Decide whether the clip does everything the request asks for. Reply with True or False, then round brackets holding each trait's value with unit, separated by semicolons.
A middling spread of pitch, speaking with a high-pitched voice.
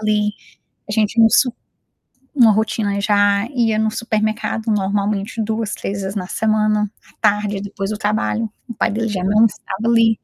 False (1.5 semitones; 215 Hz)